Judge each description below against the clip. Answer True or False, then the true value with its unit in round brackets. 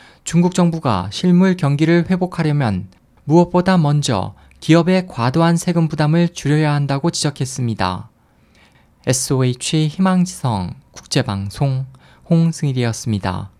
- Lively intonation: True (6.6 semitones)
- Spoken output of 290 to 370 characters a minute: False (280 characters per minute)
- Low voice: False (145 Hz)